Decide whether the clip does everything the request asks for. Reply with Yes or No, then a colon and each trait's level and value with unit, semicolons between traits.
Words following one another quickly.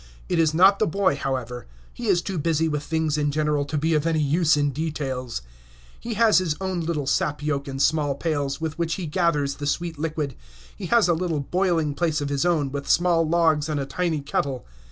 Yes: fast, 215 wpm